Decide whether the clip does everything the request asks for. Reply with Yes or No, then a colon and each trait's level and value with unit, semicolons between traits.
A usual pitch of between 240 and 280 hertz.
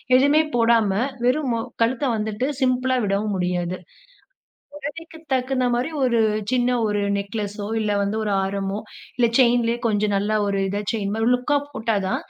No: high, 230 Hz